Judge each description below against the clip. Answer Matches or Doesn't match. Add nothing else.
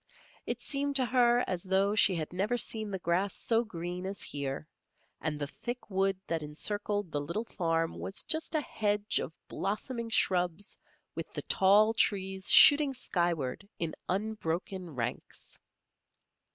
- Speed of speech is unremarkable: Matches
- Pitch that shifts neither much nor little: Matches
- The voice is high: Matches